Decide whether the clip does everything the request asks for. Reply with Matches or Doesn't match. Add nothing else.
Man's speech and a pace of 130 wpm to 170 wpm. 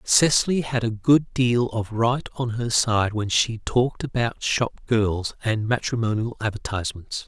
Matches